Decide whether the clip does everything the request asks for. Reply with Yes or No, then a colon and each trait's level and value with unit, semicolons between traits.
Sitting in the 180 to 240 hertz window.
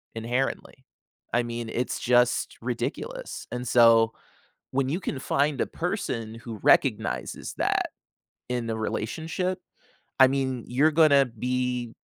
No: low, 125 Hz